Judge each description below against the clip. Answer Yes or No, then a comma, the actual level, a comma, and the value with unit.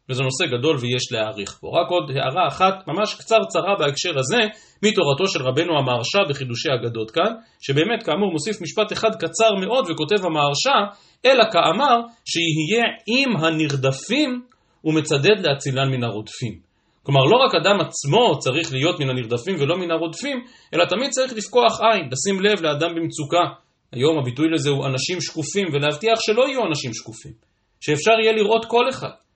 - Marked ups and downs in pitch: Yes, wide, 7.7 semitones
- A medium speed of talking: No, fast, 155 wpm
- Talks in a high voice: No, medium, 165 Hz